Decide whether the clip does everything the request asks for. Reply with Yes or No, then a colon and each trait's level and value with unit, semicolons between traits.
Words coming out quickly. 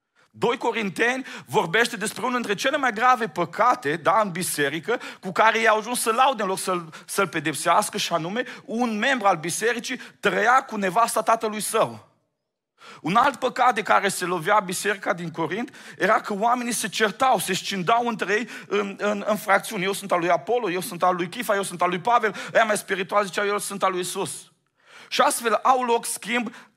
Yes: fast, 195 wpm